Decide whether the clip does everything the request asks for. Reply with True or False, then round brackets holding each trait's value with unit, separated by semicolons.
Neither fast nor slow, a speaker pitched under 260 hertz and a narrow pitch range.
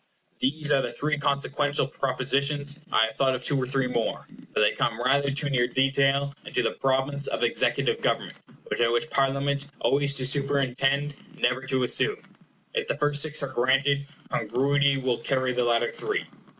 True (180 wpm; 135 Hz; 1.7 semitones)